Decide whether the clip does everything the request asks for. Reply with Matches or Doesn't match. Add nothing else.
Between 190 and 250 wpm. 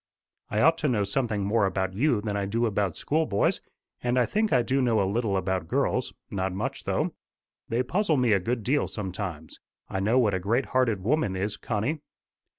Matches